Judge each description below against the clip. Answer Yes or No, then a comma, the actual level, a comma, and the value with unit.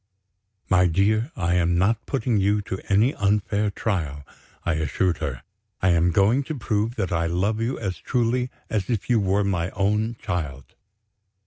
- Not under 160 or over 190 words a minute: Yes, average, 170 wpm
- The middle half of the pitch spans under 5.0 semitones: Yes, average, 3.9 semitones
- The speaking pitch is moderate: No, low, 100 Hz